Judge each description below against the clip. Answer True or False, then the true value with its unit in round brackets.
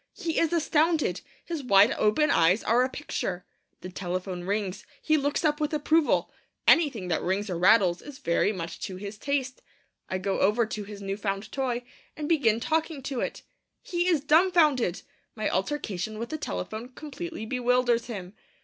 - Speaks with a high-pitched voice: True (235 Hz)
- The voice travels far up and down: True (7.2 semitones)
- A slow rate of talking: False (170 wpm)